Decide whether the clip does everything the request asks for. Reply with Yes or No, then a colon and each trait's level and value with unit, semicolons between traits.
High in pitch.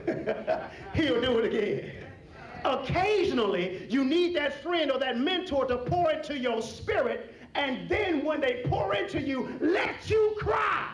Yes: very high, 295 Hz